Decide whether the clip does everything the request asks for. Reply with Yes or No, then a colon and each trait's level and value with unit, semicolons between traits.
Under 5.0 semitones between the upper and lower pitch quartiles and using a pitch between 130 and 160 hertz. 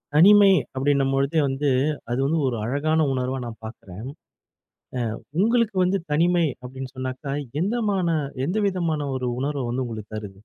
No: wide, 5.5 semitones; medium, 140 Hz